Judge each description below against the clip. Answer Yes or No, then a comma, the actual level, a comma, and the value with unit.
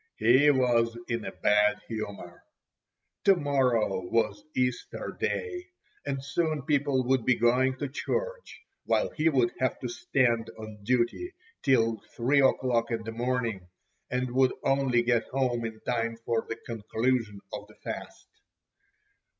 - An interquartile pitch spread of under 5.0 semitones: Yes, average, 2.7 semitones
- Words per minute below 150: Yes, average, 140 wpm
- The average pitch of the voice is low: Yes, low, 125 Hz